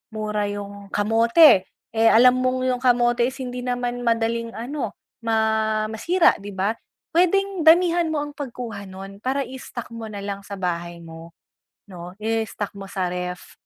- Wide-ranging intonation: No, average, 4.1 semitones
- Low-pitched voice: No, high, 225 Hz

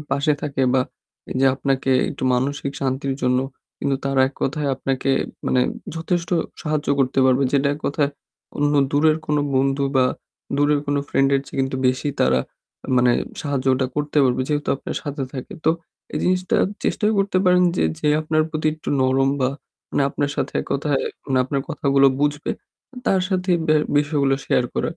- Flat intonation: Yes, narrow, 2.1 semitones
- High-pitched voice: No, medium, 140 Hz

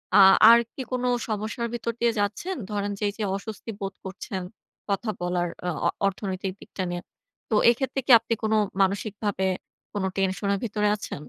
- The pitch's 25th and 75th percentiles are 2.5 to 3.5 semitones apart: Yes, average, 2.8 semitones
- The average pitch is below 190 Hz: No, high, 205 Hz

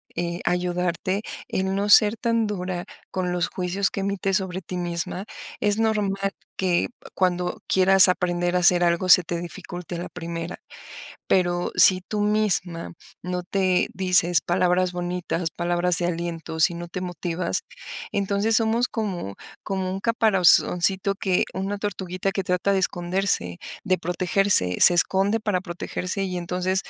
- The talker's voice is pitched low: No, medium, 180 Hz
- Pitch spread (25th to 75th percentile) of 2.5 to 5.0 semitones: No, narrow, 1.9 semitones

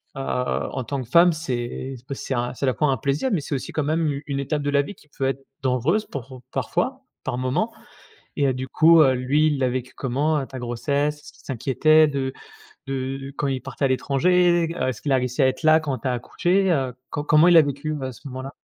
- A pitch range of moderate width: Yes, average, 3.0 semitones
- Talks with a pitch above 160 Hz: No, medium, 140 Hz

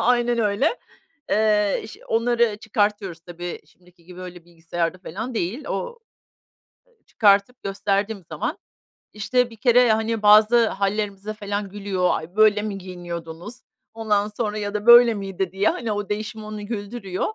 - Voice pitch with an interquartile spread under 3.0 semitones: Yes, narrow, 2.5 semitones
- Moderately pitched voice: No, high, 210 Hz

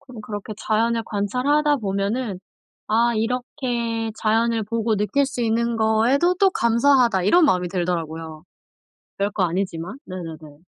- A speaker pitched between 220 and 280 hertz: Yes, high, 225 Hz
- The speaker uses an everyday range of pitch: Yes, average, 3.9 semitones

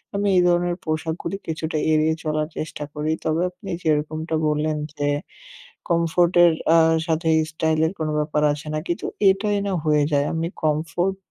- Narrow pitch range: Yes, narrow, 2.1 semitones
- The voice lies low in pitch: No, medium, 160 Hz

